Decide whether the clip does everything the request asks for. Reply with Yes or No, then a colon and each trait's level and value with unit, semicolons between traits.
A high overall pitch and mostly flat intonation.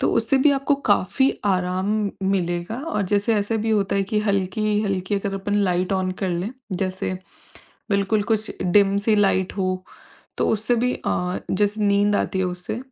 Yes: high, 200 Hz; narrow, 2.2 semitones